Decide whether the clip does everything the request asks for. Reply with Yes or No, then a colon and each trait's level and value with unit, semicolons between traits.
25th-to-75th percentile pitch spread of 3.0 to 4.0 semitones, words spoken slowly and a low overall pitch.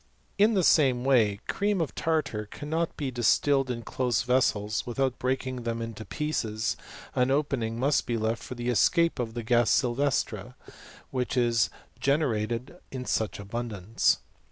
No: average, 3.3 semitones; average, 160 wpm; low, 125 Hz